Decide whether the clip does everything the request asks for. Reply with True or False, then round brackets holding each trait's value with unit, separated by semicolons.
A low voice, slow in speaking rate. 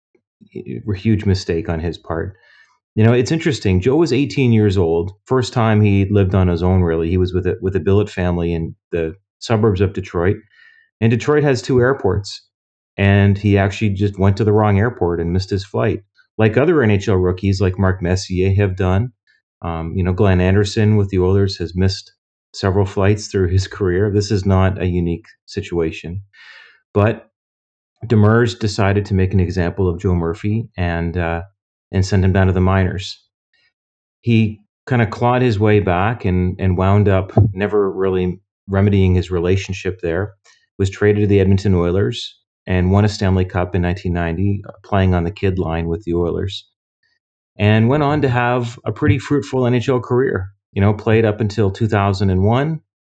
False (100 Hz; 180 wpm)